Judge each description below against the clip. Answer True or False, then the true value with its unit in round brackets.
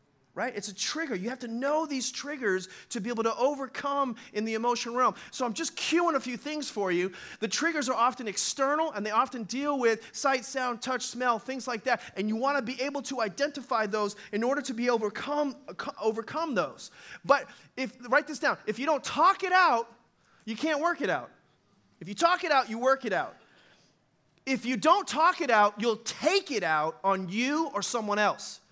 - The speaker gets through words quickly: True (210 wpm)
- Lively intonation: False (4.3 semitones)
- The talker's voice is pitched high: True (250 Hz)